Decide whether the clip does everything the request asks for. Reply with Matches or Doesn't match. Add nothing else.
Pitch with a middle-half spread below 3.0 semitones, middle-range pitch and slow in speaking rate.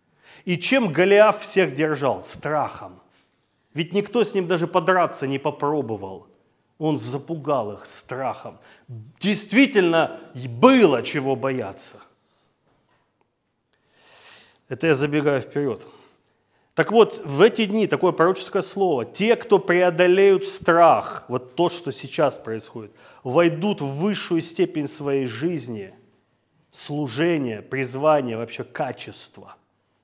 Doesn't match